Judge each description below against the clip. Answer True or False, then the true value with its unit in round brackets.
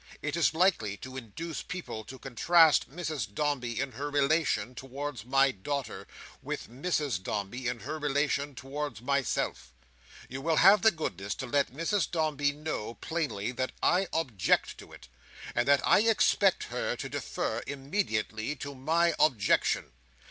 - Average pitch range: True (4.5 semitones)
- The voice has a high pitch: False (140 Hz)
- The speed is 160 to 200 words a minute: False (150 wpm)